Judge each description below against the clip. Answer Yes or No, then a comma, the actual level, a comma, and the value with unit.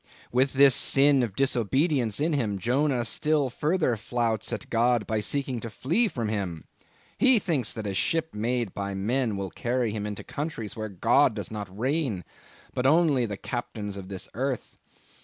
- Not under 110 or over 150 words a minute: No, average, 175 wpm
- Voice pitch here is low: Yes, low, 120 Hz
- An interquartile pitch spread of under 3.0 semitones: No, average, 4.8 semitones